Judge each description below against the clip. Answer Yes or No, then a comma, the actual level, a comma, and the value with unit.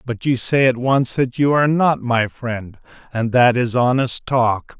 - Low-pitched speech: Yes, low, 125 Hz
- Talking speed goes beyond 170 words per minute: Yes, average, 200 wpm